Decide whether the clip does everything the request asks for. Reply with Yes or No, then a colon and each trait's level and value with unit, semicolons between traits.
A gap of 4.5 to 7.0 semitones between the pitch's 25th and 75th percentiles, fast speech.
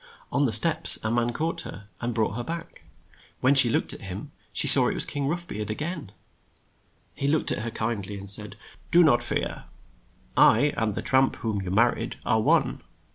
Yes: average, 4.9 semitones; fast, 210 wpm